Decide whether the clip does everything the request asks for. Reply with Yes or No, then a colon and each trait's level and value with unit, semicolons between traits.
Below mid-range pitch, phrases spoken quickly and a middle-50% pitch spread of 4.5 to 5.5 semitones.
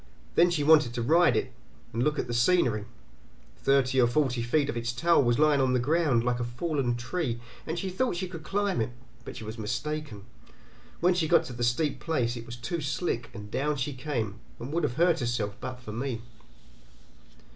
Yes: low, 130 Hz; fast, 210 wpm; average, 4.8 semitones